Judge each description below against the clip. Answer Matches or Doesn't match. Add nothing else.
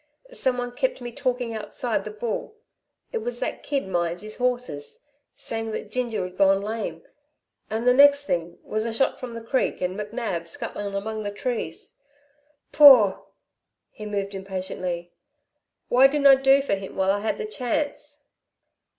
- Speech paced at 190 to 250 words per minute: Doesn't match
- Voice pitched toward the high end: Matches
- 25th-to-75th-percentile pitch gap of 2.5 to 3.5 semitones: Doesn't match